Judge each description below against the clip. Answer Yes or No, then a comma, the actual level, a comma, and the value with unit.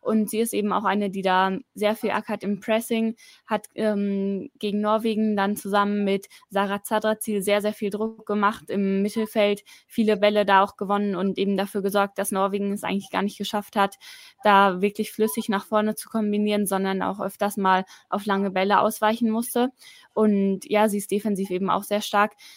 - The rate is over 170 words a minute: Yes, fast, 190 wpm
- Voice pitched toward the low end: No, high, 205 Hz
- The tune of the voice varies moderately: No, narrow, 1.4 semitones